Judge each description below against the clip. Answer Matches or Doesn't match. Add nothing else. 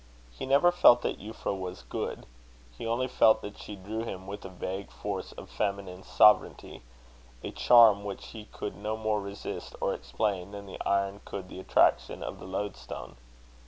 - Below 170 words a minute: Doesn't match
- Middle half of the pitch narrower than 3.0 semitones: Matches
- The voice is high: Doesn't match